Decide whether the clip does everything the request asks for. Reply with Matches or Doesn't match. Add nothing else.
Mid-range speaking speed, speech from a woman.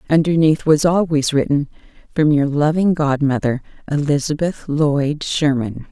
Doesn't match